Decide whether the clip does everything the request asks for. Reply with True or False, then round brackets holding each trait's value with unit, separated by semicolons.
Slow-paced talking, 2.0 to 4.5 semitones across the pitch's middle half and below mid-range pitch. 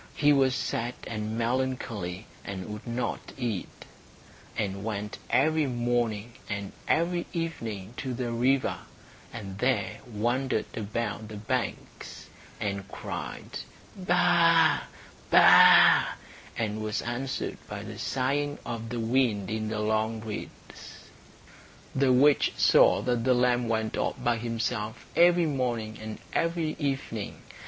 True (125 wpm; 3.6 semitones; 120 Hz)